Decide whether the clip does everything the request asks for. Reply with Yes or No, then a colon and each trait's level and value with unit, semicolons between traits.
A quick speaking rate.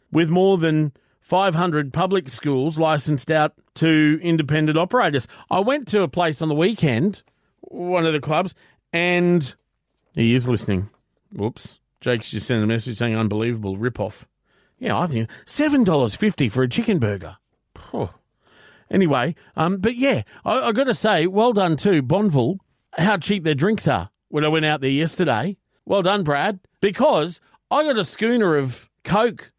No: average, 160 wpm